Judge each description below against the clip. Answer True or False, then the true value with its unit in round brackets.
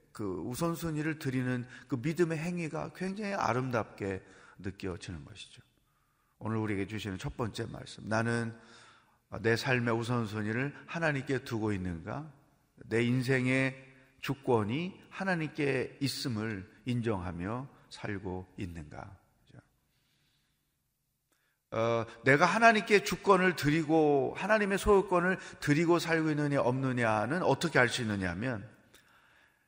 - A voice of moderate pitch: False (130 Hz)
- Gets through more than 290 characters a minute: False (260 characters per minute)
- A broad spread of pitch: True (5.8 semitones)